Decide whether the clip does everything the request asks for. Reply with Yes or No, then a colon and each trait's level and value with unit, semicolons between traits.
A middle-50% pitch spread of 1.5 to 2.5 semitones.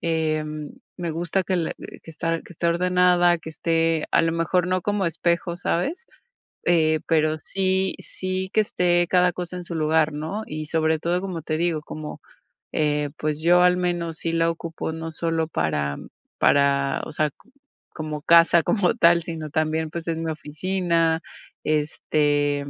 Yes: narrow, 2.1 semitones